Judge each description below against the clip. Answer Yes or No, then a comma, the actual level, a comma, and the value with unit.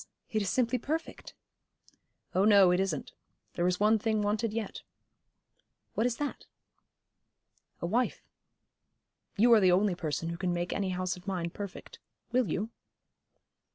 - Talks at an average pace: Yes, average, 150 wpm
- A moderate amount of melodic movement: Yes, average, 3.7 semitones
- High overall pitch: Yes, high, 200 Hz